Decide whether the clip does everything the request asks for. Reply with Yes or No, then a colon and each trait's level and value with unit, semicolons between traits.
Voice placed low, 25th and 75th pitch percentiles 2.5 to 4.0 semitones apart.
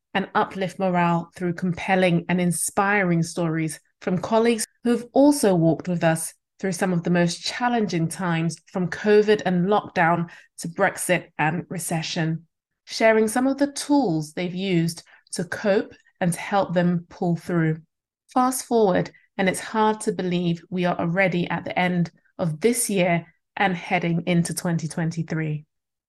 No: medium, 180 Hz; average, 3.0 semitones